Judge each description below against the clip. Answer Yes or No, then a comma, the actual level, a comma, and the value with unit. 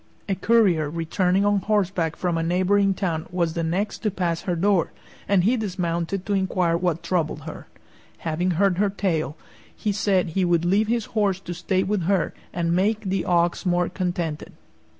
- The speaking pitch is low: No, medium, 180 Hz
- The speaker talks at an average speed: Yes, average, 180 wpm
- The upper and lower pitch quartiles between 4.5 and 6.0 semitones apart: No, average, 2.8 semitones